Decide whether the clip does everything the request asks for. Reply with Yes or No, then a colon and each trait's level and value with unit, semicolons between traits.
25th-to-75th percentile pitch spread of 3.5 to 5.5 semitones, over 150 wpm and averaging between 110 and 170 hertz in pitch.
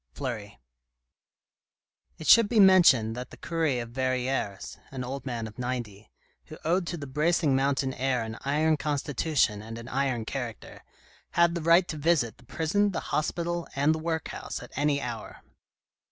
Yes: average, 4.8 semitones; average, 170 wpm; medium, 140 Hz